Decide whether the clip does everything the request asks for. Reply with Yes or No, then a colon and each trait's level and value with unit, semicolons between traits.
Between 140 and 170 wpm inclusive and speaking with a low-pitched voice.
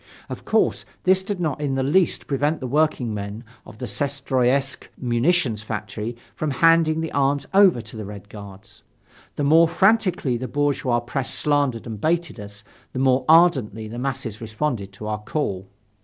Yes: average, 165 wpm; low, 130 Hz